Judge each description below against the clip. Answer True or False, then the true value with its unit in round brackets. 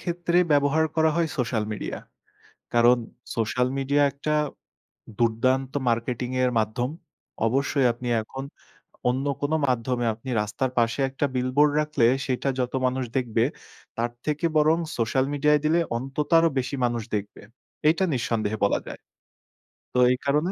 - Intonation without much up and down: False (3.5 semitones)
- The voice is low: True (130 Hz)